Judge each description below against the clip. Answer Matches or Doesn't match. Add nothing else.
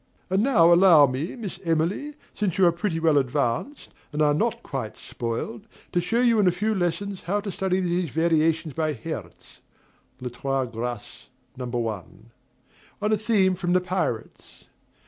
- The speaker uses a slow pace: Doesn't match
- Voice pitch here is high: Doesn't match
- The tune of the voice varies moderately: Doesn't match